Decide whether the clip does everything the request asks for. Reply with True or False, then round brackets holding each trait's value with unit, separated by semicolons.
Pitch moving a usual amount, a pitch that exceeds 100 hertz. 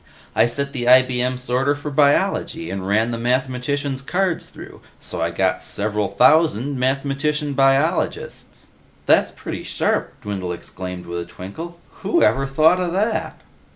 True (4.3 semitones; 135 Hz)